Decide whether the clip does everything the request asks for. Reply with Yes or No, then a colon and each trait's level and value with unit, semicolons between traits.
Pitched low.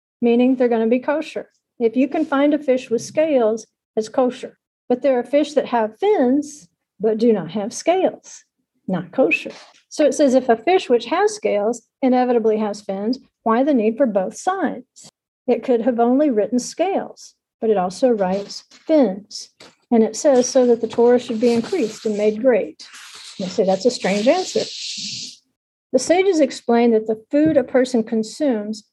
No: high, 245 Hz